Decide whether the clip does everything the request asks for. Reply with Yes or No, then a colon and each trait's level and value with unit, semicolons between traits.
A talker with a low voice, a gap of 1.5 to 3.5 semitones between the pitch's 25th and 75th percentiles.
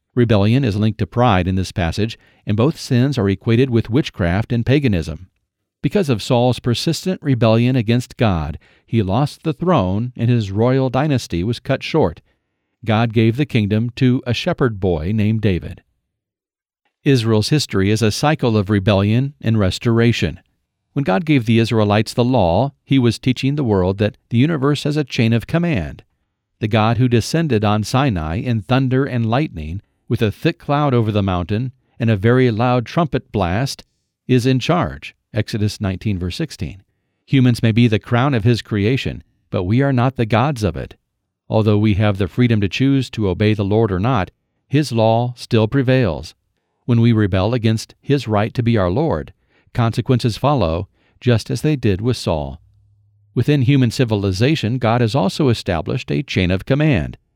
No: low, 115 Hz; average, 4.0 semitones